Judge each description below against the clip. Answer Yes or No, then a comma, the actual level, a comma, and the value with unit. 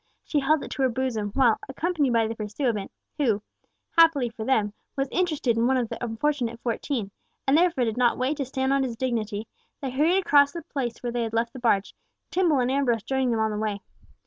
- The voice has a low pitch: No, very high, 250 Hz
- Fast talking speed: Yes, fast, 210 wpm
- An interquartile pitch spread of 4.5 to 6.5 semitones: No, average, 3.6 semitones